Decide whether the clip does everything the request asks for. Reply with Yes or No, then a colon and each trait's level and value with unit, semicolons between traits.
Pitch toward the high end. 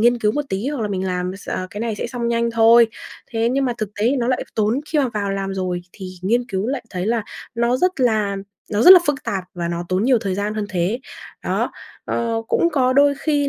Yes: high, 225 Hz